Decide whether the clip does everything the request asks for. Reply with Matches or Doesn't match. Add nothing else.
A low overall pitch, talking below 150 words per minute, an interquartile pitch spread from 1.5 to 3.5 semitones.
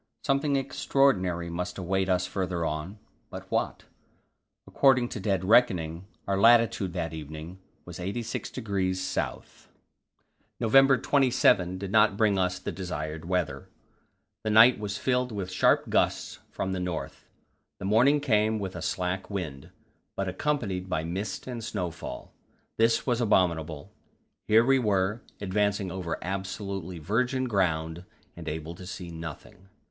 Doesn't match